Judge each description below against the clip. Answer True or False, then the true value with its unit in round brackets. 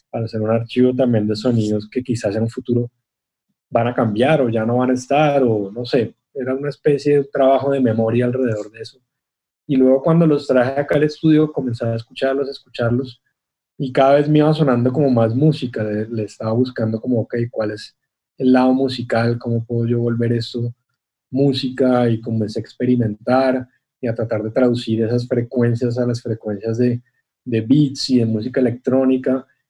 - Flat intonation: True (2.3 semitones)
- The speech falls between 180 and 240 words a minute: True (190 wpm)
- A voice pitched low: True (125 Hz)